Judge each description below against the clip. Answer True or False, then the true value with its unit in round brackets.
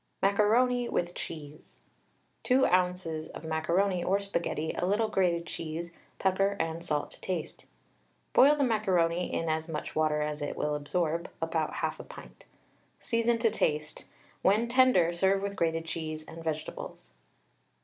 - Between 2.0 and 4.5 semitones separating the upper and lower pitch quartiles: True (4.0 semitones)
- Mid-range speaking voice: True (170 Hz)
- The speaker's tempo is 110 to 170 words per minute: True (145 wpm)